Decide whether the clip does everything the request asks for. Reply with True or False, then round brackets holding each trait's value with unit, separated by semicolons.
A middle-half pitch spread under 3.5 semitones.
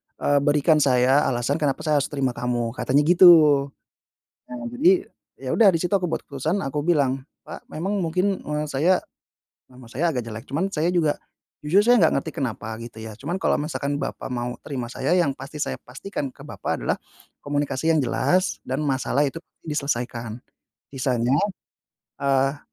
False (4.1 semitones)